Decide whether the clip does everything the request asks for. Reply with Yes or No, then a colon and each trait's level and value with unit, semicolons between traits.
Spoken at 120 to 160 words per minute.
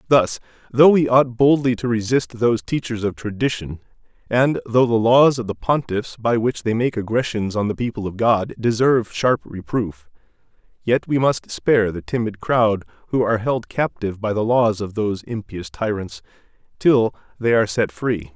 No: average, 175 wpm